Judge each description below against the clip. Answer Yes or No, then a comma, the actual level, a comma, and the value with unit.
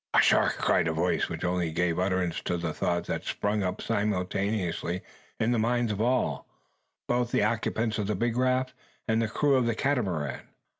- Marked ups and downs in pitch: No, average, 4.8 semitones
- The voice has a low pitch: Yes, low, 105 Hz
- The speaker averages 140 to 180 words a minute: No, average, 190 wpm